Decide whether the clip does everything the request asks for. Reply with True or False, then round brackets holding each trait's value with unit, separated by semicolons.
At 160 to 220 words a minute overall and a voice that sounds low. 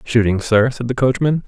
True (205 wpm; 120 Hz)